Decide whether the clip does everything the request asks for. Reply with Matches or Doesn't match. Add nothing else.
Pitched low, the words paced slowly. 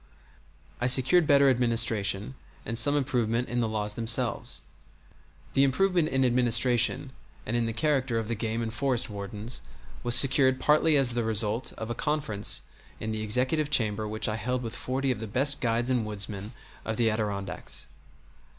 Doesn't match